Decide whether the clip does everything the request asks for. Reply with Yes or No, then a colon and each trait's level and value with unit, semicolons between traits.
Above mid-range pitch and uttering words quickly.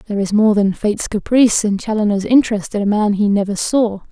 Yes: high, 210 Hz; fast, 220 wpm